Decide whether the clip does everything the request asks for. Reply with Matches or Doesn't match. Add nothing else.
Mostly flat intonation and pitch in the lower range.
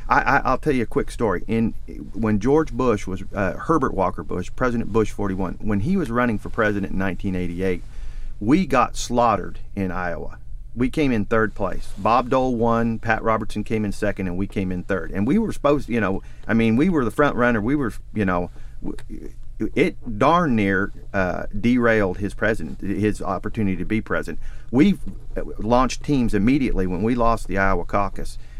Doesn't match